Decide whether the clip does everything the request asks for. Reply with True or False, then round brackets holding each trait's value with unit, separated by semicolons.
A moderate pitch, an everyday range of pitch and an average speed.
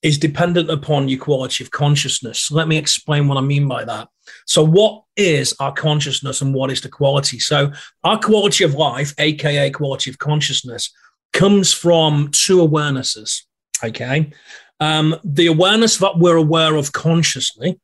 True (150 Hz; 3.1 semitones; 160 wpm)